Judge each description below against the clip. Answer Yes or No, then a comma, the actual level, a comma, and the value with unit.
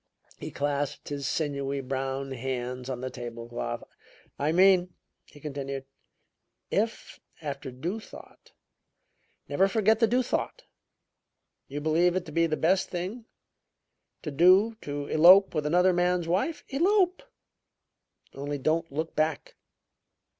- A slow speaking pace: Yes, slow, 130 wpm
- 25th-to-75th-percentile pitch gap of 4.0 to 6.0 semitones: Yes, average, 5.2 semitones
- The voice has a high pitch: No, medium, 155 Hz